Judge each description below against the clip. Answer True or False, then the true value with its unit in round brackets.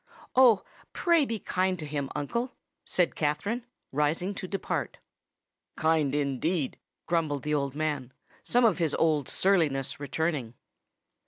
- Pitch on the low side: False (160 Hz)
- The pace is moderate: False (120 wpm)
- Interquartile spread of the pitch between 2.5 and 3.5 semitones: False (4.7 semitones)